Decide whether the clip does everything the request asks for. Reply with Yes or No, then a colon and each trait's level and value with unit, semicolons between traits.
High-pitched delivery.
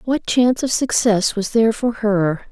Yes: high, 225 Hz